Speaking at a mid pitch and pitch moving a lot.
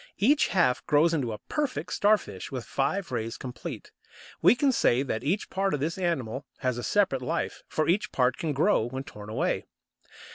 Yes: medium, 145 Hz; wide, 7.4 semitones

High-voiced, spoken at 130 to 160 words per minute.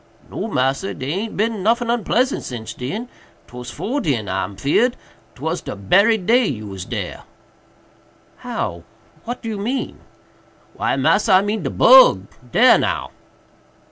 Yes: high, 195 Hz; slow, 135 wpm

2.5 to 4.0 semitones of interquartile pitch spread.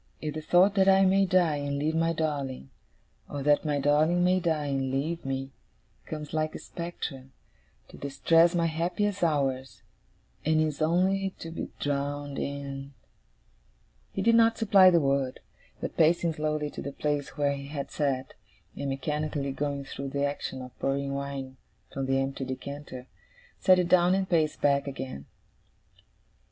Yes: average, 3.3 semitones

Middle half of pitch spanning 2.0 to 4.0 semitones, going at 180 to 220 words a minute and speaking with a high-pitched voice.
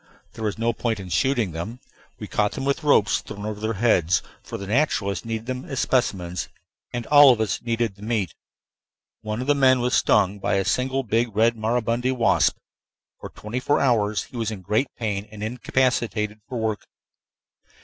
No: average, 3.2 semitones; average, 190 wpm; low, 115 Hz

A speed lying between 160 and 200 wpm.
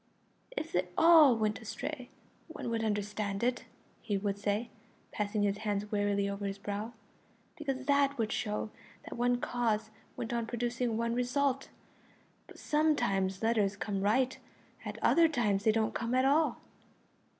No: average, 150 wpm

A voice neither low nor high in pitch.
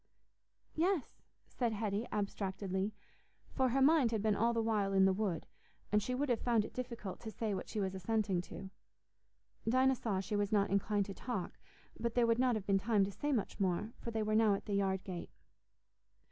No: high, 215 Hz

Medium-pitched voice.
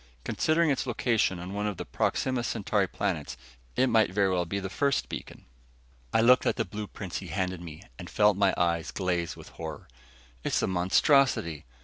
No: low, 100 Hz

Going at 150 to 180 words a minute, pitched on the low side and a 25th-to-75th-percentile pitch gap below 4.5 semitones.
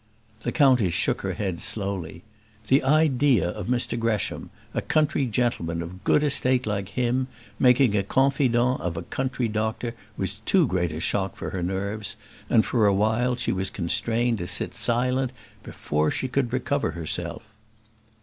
No: average, 160 wpm; low, 115 Hz; average, 5.1 semitones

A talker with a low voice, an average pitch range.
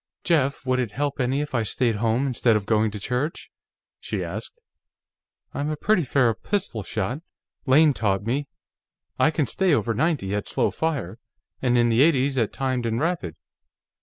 Yes: low, 130 Hz; average, 4.5 semitones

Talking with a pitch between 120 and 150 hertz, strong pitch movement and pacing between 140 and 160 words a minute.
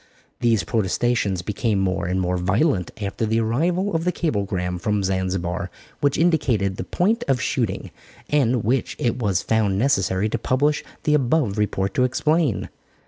No: low, 110 Hz; wide, 6.2 semitones; average, 155 wpm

